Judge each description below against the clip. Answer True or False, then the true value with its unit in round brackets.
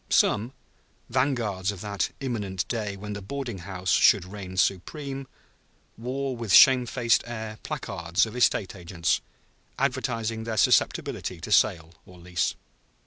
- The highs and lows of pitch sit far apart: False (4.3 semitones)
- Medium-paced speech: False (130 wpm)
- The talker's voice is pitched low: True (105 Hz)